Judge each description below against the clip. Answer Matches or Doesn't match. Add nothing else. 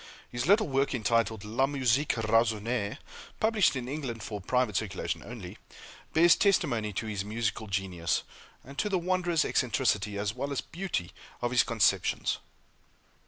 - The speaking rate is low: Doesn't match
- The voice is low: Matches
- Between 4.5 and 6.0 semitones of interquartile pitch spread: Matches